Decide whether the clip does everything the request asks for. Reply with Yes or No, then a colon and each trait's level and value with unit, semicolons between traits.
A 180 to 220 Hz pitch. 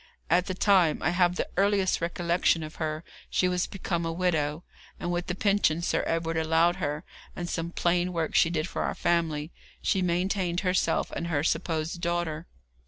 No: medium, 170 Hz